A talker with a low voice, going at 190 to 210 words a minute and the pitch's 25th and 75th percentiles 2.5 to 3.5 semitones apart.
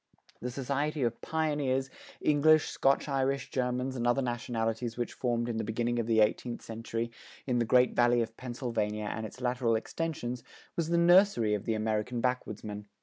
No: low, 120 Hz; average, 170 wpm; average, 2.9 semitones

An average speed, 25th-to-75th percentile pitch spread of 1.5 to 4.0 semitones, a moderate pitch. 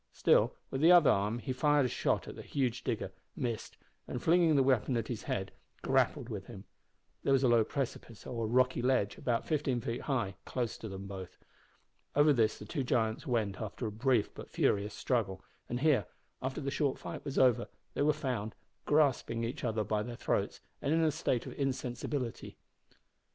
No: average, 190 wpm; average, 3.6 semitones; low, 125 Hz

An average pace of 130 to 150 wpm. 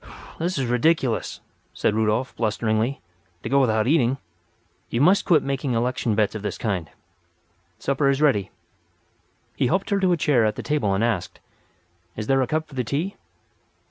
No: average, 175 wpm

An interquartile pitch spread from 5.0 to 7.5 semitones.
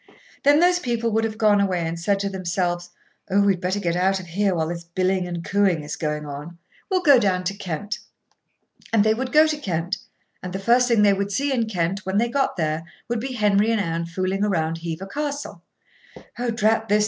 No: average, 4.3 semitones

